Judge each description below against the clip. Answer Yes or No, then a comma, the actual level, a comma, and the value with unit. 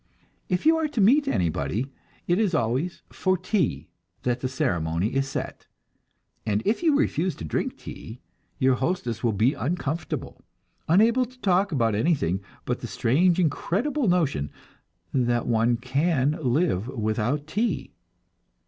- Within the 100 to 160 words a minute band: Yes, average, 140 wpm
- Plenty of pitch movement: Yes, wide, 8.1 semitones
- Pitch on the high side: No, medium, 140 Hz